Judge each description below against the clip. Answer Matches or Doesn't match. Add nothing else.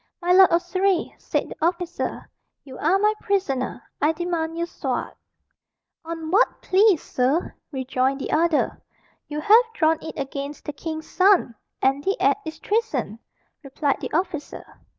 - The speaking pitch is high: Matches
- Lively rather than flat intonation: Doesn't match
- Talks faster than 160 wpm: Doesn't match